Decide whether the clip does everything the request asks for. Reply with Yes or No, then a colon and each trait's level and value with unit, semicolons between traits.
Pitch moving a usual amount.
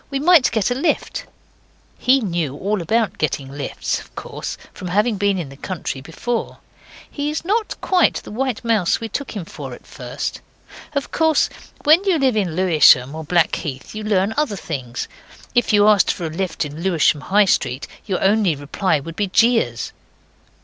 No: wide, 7.0 semitones